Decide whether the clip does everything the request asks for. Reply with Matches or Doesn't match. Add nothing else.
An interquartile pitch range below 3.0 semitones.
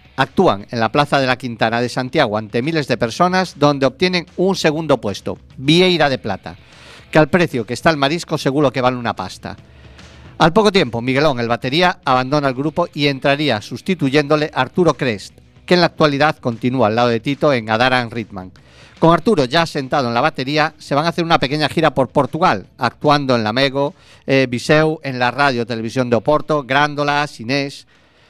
Doesn't match